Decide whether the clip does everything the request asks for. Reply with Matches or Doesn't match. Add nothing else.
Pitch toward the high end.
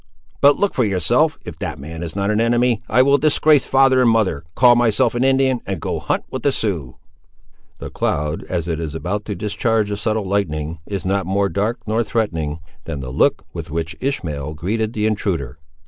Doesn't match